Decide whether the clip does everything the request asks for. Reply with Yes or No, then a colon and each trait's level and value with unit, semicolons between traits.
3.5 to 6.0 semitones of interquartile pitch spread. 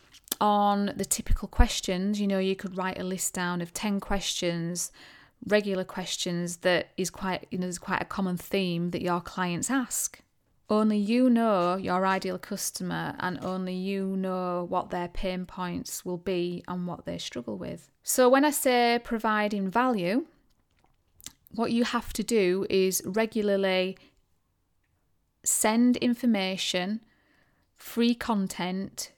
No: average, 3.1 semitones